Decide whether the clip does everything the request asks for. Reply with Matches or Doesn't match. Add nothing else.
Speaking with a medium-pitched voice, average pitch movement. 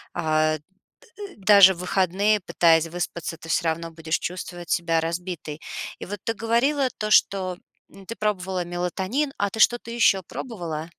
Matches